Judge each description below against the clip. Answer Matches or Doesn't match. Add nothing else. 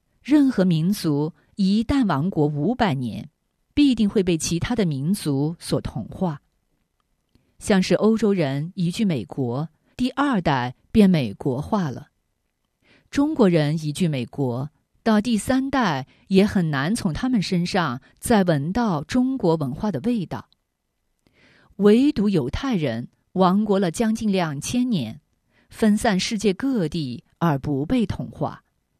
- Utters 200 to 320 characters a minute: Doesn't match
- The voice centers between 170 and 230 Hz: Matches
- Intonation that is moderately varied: Doesn't match